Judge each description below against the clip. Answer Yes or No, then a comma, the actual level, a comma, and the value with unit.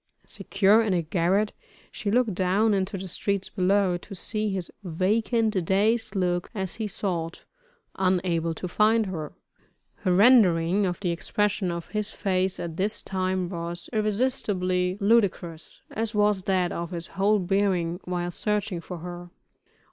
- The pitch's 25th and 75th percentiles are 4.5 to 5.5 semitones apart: No, average, 2.9 semitones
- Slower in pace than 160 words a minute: Yes, average, 150 wpm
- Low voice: No, high, 190 Hz